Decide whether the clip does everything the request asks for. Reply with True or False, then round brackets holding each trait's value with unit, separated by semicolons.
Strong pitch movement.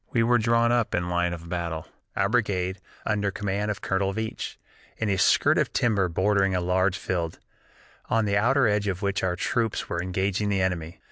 False (2.8 semitones)